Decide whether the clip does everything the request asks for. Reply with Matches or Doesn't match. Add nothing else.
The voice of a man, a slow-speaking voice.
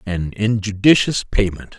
Matches